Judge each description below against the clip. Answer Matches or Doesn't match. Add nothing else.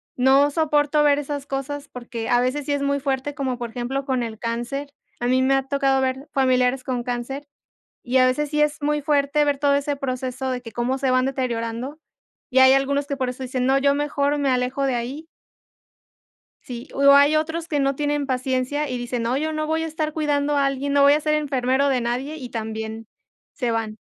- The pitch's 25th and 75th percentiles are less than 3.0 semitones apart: Matches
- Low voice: Doesn't match